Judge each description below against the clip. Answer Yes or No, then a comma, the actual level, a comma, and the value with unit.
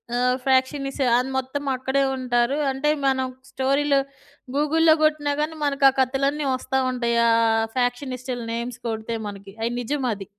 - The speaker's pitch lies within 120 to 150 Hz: No, very high, 260 Hz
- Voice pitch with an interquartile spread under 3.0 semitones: Yes, narrow, 2.4 semitones